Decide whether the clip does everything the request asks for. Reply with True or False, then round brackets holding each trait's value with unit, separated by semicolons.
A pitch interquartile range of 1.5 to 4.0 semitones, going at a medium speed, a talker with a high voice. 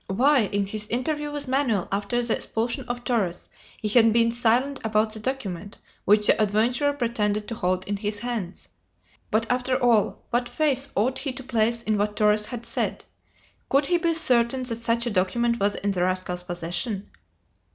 True (3.3 semitones; 185 wpm; 230 Hz)